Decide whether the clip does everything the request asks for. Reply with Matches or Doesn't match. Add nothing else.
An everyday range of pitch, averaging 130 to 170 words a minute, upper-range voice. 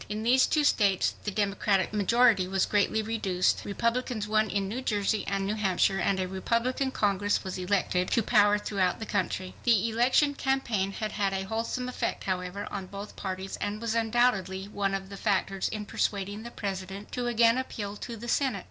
Doesn't match